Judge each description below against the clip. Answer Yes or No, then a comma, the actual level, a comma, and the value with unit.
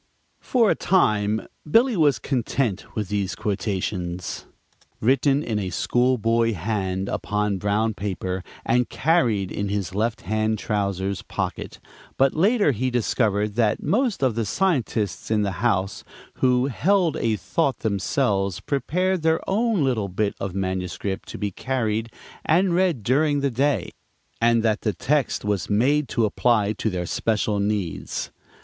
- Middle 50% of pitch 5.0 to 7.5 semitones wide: Yes, average, 5.3 semitones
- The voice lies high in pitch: No, low, 110 Hz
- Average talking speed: Yes, average, 145 wpm